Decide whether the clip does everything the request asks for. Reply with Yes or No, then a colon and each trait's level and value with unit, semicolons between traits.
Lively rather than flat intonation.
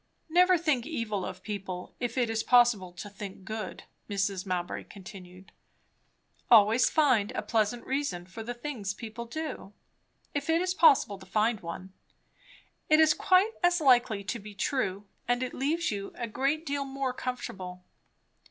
Yes: wide, 6.0 semitones